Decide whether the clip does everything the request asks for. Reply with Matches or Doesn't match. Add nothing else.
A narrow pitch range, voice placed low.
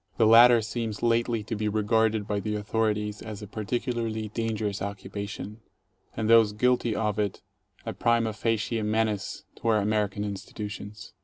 Matches